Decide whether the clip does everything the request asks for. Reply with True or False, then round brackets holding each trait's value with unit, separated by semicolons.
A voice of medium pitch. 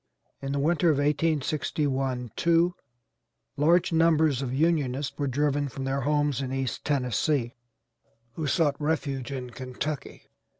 True (145 Hz)